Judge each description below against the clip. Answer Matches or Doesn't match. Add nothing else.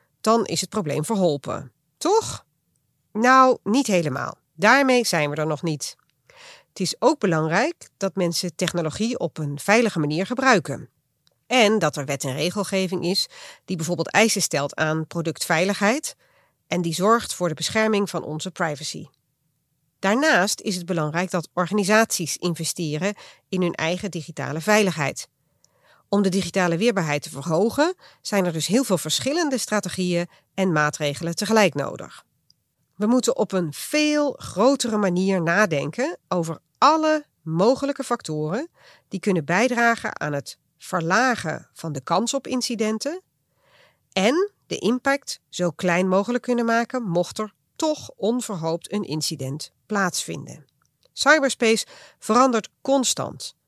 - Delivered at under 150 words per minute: Matches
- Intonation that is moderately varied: Doesn't match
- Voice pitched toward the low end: Doesn't match